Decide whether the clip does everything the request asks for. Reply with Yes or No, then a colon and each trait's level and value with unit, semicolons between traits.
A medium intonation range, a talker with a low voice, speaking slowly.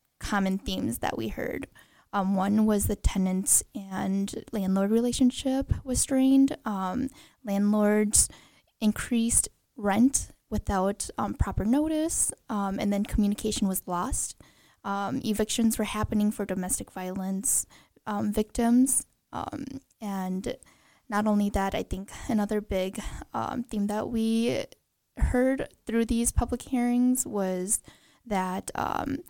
No: average, 3.6 semitones; high, 215 Hz; slow, 120 wpm